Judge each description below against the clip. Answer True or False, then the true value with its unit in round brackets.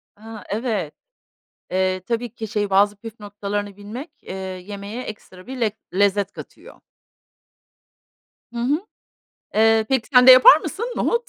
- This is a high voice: True (215 Hz)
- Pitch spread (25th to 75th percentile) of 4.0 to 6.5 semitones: False (3.2 semitones)